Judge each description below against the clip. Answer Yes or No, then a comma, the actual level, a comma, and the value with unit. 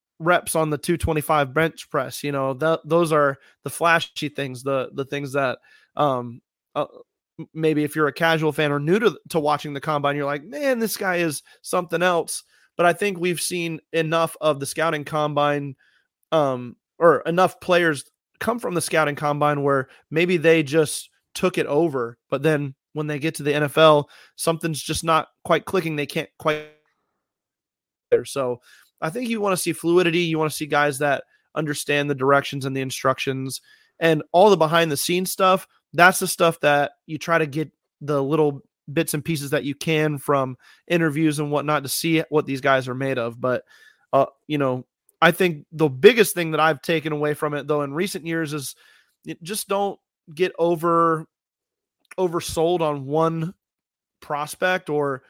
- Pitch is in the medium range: Yes, medium, 155 Hz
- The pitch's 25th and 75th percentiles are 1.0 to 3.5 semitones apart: Yes, average, 2.7 semitones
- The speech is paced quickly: No, average, 180 wpm